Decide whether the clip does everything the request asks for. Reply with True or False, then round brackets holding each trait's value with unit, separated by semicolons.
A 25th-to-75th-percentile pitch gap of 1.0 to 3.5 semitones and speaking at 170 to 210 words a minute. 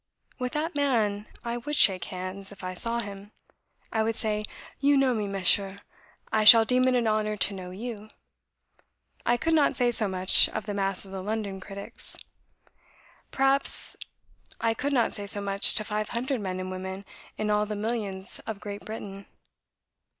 True (3.2 semitones; 180 wpm)